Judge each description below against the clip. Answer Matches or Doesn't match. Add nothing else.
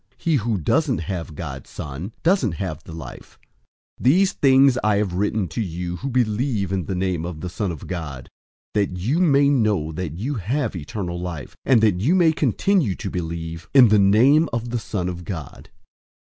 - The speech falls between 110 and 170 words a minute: Doesn't match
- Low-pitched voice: Matches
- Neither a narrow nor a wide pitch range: Doesn't match